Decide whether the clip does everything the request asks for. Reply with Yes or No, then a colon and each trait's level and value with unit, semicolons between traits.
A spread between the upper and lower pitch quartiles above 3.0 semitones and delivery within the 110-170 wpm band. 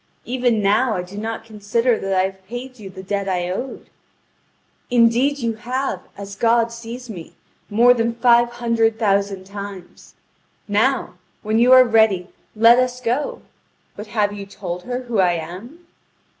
Yes: average, 3.4 semitones; average, 160 wpm